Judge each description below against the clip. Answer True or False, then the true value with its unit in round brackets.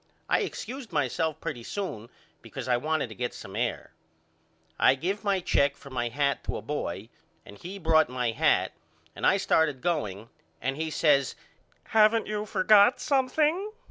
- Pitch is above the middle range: False (155 Hz)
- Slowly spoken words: False (165 wpm)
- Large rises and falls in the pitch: True (8.4 semitones)